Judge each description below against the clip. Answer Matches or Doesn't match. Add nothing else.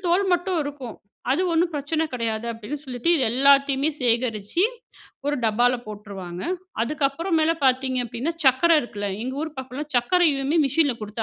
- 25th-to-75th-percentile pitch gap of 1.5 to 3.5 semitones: Doesn't match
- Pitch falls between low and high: Doesn't match